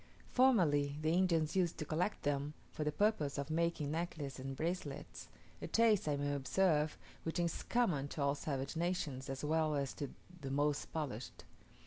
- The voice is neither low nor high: Yes, medium, 150 Hz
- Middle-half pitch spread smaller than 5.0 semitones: Yes, average, 3.3 semitones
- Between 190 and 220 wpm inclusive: No, average, 170 wpm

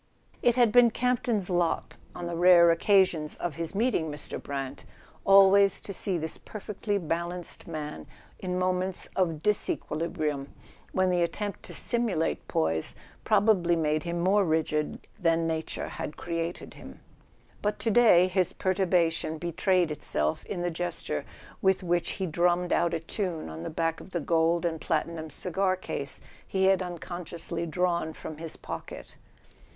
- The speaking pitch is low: No, medium, 175 Hz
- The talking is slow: No, average, 155 wpm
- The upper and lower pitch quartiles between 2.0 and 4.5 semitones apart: Yes, average, 2.8 semitones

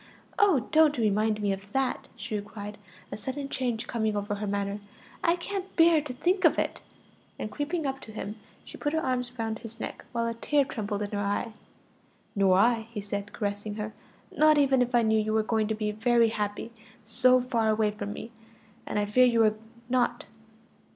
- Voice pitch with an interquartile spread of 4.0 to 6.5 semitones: No, average, 3.5 semitones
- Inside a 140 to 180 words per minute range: No, average, 200 wpm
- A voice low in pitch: No, high, 225 Hz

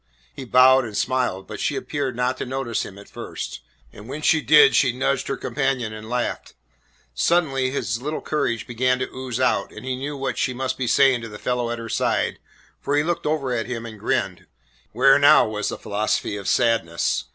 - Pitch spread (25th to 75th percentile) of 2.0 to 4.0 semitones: Yes, average, 2.8 semitones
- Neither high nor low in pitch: No, low, 125 Hz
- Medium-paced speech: No, fast, 210 wpm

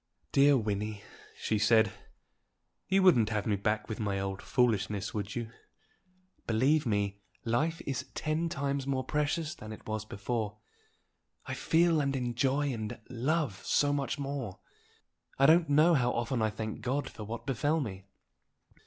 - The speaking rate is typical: Yes, average, 155 wpm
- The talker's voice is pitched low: Yes, low, 120 Hz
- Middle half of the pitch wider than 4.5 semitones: Yes, average, 5.1 semitones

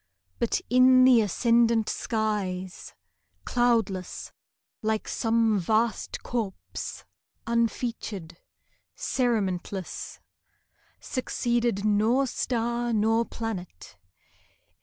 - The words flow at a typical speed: No, slow, 70 wpm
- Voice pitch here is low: No, high, 225 Hz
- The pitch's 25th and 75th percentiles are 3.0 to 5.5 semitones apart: No, narrow, 2.6 semitones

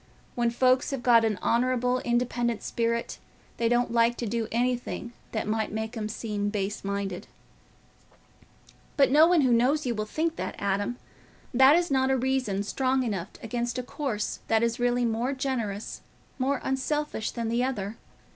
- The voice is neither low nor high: No, high, 240 Hz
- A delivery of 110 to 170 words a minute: Yes, average, 165 wpm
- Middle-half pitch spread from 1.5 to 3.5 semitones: Yes, average, 2.8 semitones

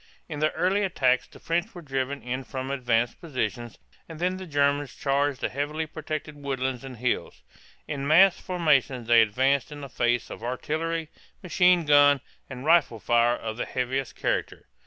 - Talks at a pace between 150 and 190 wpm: Yes, average, 170 wpm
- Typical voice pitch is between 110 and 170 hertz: Yes, medium, 140 Hz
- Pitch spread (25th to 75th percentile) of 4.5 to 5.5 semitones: No, average, 3.8 semitones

